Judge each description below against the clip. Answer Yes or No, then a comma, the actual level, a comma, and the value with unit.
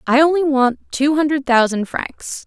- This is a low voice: No, very high, 275 Hz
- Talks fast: No, average, 170 wpm